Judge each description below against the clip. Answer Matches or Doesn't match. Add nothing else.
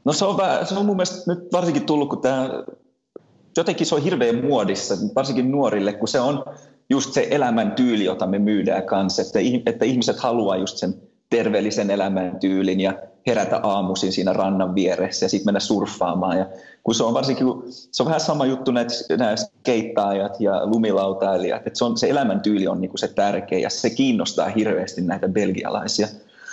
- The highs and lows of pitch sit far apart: Matches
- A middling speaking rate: Doesn't match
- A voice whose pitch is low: Matches